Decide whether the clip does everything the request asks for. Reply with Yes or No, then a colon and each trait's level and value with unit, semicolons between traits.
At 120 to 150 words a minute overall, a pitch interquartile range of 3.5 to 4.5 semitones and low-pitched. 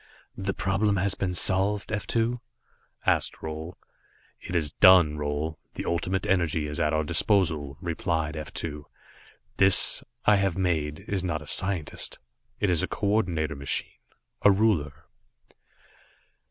Yes: average, 140 wpm; average, 4.1 semitones; very low, 85 Hz